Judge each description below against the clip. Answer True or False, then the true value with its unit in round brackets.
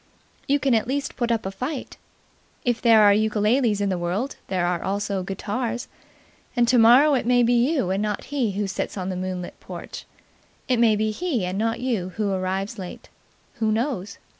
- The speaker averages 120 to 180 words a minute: False (190 wpm)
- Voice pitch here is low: False (215 Hz)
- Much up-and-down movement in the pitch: False (4.0 semitones)